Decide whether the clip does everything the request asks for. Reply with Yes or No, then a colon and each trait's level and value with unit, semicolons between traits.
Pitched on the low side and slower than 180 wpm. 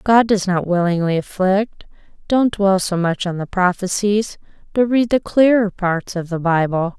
No: high, 195 Hz; average, 170 wpm